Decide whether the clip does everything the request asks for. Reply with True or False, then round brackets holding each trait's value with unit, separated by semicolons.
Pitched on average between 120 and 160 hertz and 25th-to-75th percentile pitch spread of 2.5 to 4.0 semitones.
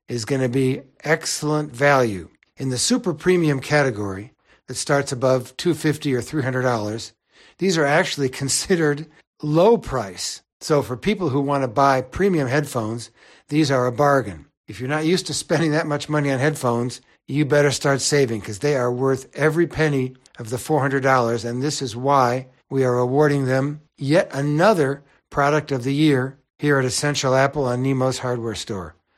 True (140 Hz; 2.8 semitones)